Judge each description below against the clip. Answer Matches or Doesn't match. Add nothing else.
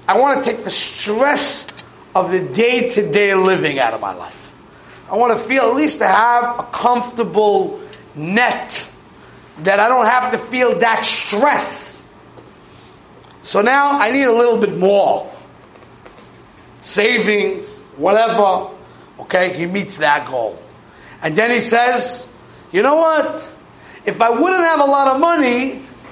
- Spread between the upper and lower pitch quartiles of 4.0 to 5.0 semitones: Matches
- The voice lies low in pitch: Doesn't match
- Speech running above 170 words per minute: Doesn't match